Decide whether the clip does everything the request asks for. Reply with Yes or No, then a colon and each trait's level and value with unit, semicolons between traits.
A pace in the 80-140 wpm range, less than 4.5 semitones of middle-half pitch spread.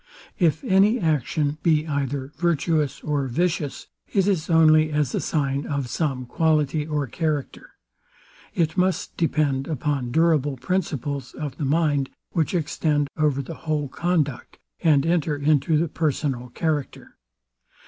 Yes: slow, 135 wpm; narrow, 2.6 semitones